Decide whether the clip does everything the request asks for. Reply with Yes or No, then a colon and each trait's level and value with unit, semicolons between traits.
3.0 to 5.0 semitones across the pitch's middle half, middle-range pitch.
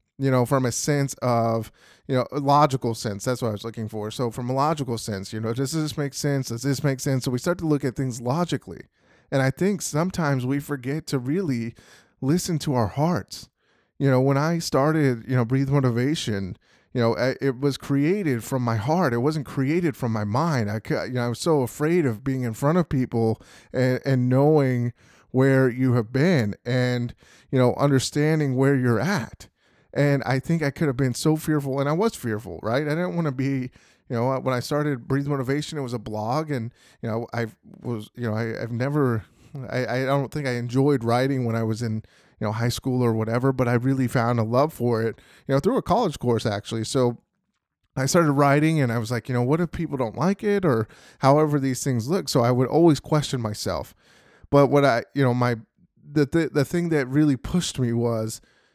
No: average, 3.6 semitones; low, 130 Hz